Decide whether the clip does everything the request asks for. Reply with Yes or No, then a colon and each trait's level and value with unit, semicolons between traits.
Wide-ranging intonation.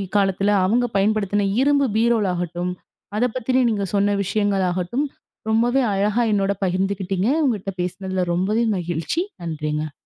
No: average, 3.4 semitones